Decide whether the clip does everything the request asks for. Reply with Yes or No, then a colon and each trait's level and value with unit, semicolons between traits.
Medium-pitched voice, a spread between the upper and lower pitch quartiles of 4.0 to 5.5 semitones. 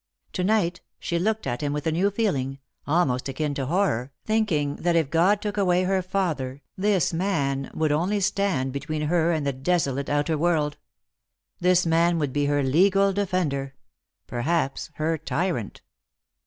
Yes: medium, 165 Hz; average, 4.6 semitones